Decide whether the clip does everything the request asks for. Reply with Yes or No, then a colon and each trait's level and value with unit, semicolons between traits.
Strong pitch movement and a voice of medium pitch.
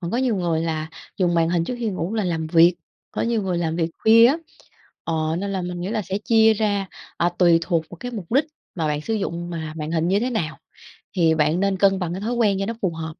No: average, 4.1 semitones; medium, 180 Hz